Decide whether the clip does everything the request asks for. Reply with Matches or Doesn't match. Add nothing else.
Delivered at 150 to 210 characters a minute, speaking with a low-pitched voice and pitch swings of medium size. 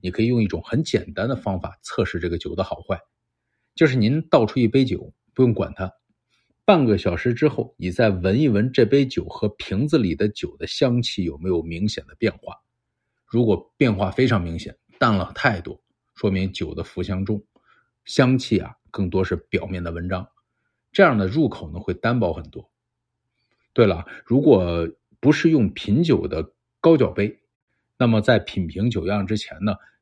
Doesn't match